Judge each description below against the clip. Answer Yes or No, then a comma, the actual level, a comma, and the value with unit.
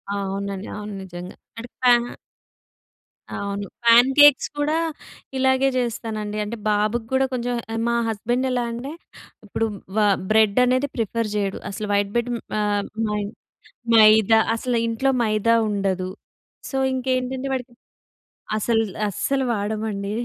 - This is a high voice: Yes, high, 225 Hz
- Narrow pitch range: No, average, 3.3 semitones